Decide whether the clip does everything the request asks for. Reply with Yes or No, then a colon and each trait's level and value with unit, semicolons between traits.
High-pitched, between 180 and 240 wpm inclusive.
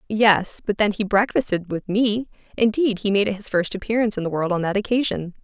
Yes: high, 205 Hz; average, 200 wpm